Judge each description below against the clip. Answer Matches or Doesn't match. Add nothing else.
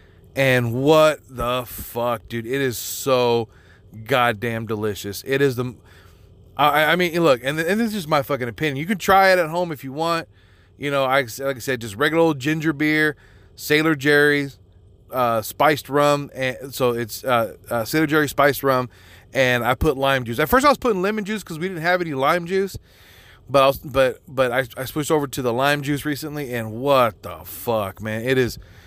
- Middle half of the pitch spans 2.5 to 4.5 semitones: Doesn't match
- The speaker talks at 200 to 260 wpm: Matches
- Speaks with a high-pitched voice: Doesn't match